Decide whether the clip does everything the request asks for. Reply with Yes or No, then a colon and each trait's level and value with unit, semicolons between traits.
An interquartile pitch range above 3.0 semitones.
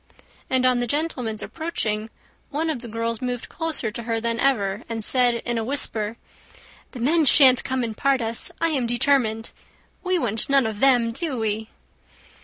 Yes: average, 3.5 semitones